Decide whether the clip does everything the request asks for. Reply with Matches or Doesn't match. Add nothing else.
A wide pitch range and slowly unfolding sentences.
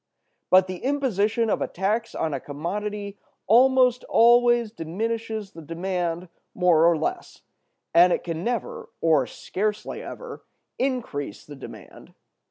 Matches